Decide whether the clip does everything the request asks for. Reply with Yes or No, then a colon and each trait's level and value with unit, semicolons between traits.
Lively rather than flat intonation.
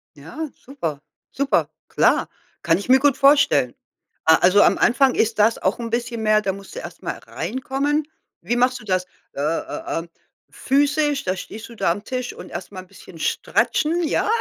Yes: wide, 6.7 semitones